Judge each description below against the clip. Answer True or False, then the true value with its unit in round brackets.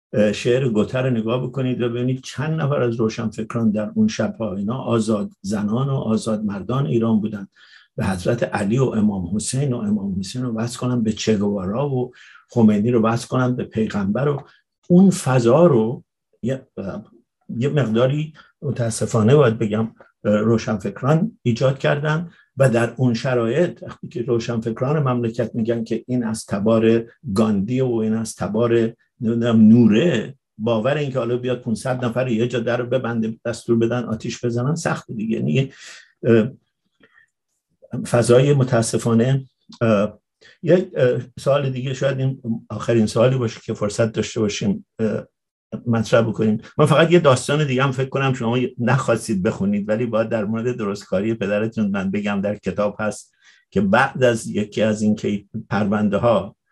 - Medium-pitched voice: False (115 Hz)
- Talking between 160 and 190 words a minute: False (150 wpm)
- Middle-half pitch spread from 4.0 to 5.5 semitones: False (2.9 semitones)